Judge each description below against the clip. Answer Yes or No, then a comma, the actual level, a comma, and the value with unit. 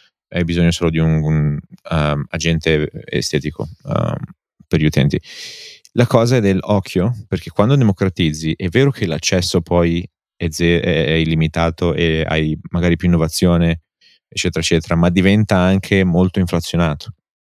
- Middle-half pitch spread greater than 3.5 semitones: No, narrow, 2.6 semitones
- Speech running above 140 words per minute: No, average, 135 wpm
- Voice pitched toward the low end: Yes, very low, 85 Hz